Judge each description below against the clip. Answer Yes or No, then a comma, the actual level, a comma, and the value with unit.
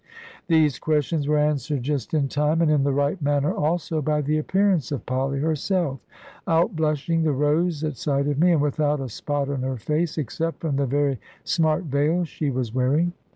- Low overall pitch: No, medium, 150 Hz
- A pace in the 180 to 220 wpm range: Yes, average, 190 wpm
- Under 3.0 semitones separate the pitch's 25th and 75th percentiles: Yes, narrow, 2.4 semitones